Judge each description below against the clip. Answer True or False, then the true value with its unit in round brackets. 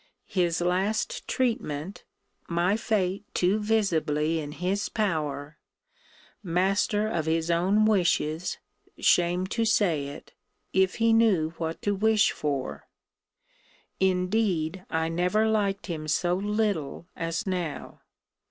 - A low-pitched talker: False (180 Hz)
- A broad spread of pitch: False (4.2 semitones)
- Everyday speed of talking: False (115 wpm)